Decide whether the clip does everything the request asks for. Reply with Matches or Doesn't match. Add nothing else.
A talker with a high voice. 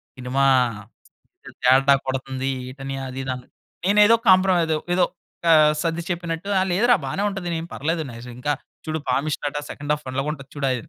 Doesn't match